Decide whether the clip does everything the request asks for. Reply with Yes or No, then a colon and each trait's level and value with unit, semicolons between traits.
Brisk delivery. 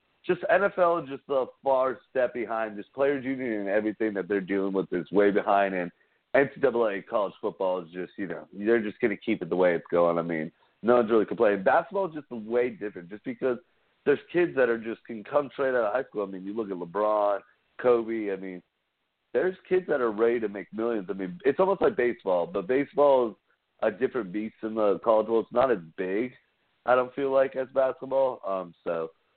Yes: fast, 220 wpm